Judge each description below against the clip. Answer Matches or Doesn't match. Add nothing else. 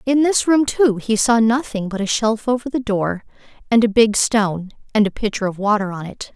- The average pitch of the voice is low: Doesn't match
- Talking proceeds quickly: Matches